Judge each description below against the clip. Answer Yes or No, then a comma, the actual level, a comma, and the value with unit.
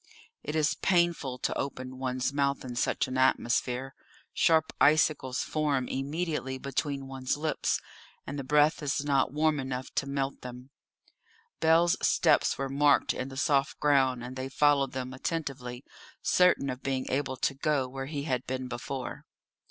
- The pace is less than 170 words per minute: Yes, average, 160 wpm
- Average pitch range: No, narrow, 2.3 semitones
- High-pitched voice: No, low, 135 Hz